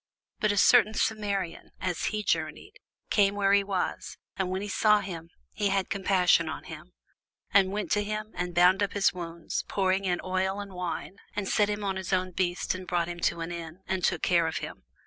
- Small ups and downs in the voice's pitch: Yes, narrow, 2.3 semitones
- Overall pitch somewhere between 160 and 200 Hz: Yes, high, 190 Hz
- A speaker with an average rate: No, fast, 210 wpm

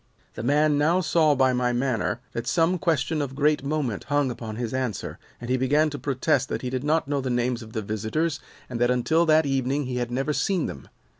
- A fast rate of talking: Yes, fast, 225 wpm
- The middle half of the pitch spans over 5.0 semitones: No, average, 3.6 semitones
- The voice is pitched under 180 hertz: Yes, low, 135 Hz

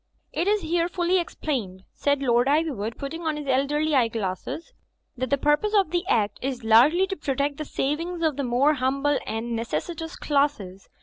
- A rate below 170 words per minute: No, average, 175 wpm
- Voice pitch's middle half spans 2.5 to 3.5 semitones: No, average, 5.0 semitones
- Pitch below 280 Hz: No, very high, 285 Hz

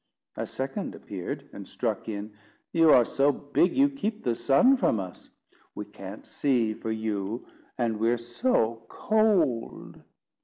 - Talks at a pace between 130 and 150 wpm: Yes, average, 145 wpm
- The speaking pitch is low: Yes, low, 120 Hz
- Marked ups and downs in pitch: Yes, wide, 7.8 semitones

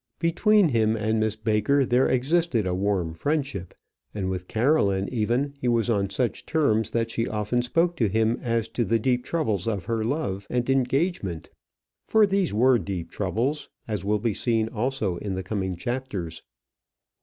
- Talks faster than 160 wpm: Yes, average, 170 wpm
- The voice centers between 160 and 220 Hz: No, low, 115 Hz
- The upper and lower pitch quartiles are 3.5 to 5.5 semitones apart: Yes, average, 4.5 semitones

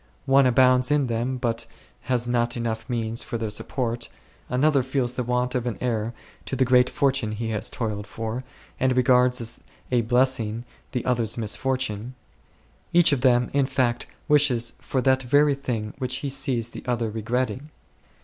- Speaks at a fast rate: No, average, 170 wpm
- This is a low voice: Yes, low, 125 Hz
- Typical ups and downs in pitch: No, narrow, 2.1 semitones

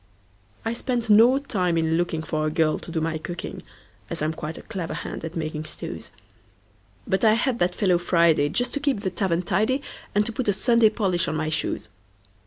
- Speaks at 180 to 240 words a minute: Yes, average, 185 wpm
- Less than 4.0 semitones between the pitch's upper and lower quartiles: No, wide, 5.6 semitones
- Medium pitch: Yes, medium, 175 Hz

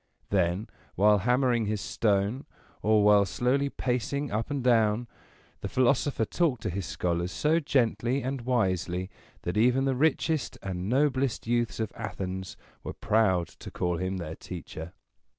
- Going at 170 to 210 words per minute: No, average, 150 wpm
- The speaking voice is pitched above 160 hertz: No, low, 110 Hz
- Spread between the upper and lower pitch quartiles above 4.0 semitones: Yes, average, 5.3 semitones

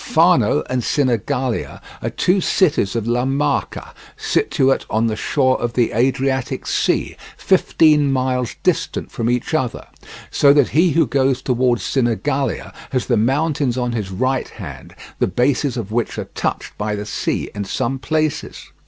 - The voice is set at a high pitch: No, low, 130 Hz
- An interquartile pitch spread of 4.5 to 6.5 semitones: No, average, 2.9 semitones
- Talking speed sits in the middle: Yes, average, 155 wpm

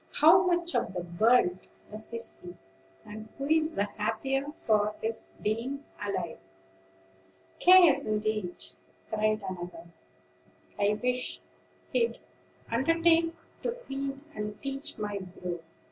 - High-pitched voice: Yes, high, 225 Hz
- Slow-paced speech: Yes, slow, 115 wpm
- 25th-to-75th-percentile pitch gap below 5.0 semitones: No, wide, 5.4 semitones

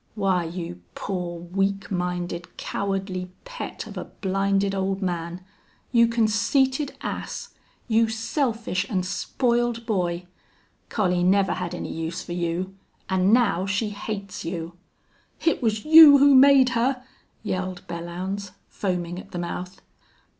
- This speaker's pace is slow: Yes, slow, 130 wpm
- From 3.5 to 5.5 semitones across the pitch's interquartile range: Yes, average, 4.1 semitones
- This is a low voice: No, high, 195 Hz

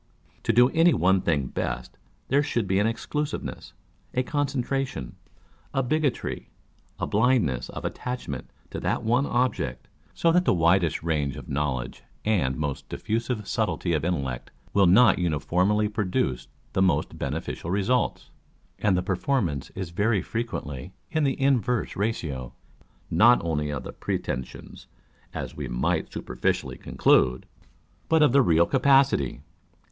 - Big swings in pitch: Yes, wide, 8.9 semitones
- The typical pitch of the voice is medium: No, very low, 95 Hz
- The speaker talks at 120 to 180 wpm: Yes, average, 140 wpm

